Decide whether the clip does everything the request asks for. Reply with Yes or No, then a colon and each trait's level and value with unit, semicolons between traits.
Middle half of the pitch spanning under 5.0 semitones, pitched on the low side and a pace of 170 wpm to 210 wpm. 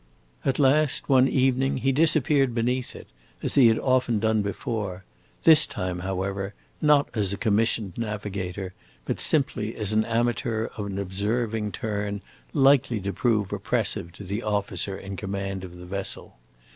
No: average, 4.5 semitones; low, 110 Hz; average, 155 wpm